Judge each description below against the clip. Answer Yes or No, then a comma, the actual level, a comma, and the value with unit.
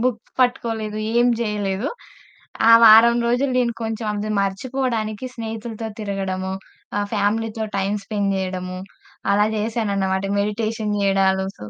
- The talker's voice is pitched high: Yes, high, 215 Hz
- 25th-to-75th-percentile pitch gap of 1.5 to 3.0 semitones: Yes, narrow, 2.4 semitones